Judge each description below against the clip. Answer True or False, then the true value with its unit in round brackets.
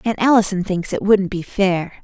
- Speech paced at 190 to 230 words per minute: True (205 wpm)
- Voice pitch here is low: False (190 Hz)